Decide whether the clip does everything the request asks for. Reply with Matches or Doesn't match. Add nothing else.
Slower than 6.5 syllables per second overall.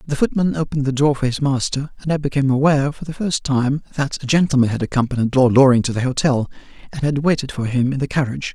Doesn't match